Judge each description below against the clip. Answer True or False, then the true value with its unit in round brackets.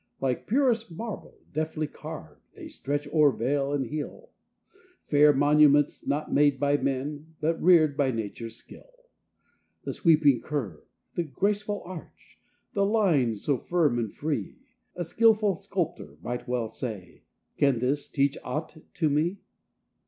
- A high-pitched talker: False (150 Hz)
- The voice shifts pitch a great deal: False (4.1 semitones)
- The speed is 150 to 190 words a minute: False (135 wpm)